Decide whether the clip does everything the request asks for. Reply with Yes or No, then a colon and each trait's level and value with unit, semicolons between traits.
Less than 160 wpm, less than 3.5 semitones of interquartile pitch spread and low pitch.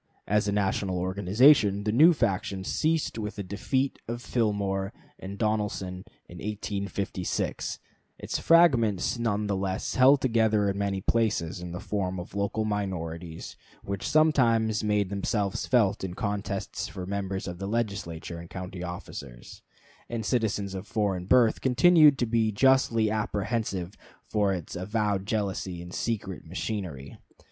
Yes: slow, 135 wpm; average, 2.9 semitones; low, 100 Hz